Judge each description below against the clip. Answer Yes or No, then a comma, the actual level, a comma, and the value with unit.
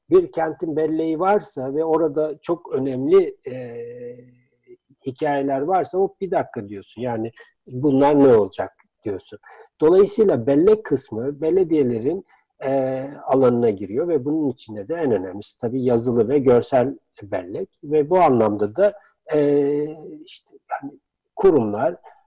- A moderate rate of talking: Yes, average, 125 wpm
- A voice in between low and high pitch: Yes, medium, 150 Hz